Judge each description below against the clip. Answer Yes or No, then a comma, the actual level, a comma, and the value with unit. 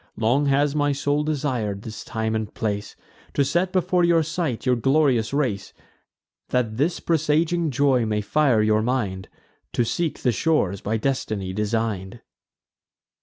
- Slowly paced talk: No, average, 145 wpm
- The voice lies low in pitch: Yes, low, 125 Hz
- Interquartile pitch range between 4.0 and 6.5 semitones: Yes, wide, 5.5 semitones